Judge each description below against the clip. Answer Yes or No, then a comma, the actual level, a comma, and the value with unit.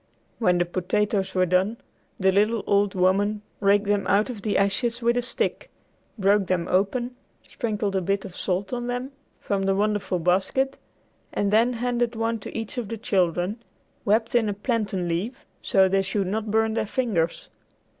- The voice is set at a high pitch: Yes, high, 205 Hz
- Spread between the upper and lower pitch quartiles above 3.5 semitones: No, average, 3.1 semitones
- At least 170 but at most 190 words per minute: Yes, average, 175 wpm